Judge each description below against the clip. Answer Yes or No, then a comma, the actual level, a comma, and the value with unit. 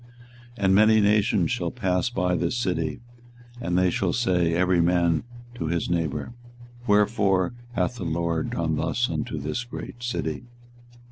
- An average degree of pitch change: Yes, average, 3.8 semitones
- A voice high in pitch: No, very low, 90 Hz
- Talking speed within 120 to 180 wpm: Yes, average, 150 wpm